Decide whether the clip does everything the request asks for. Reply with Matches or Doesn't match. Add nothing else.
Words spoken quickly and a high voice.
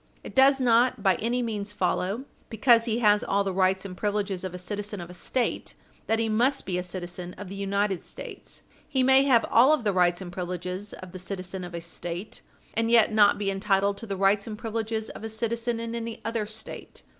Matches